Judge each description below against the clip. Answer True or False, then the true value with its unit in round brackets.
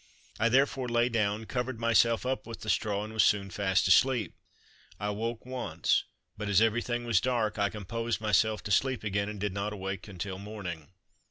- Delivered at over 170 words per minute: True (185 wpm)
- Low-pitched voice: True (110 Hz)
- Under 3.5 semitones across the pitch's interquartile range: True (2.6 semitones)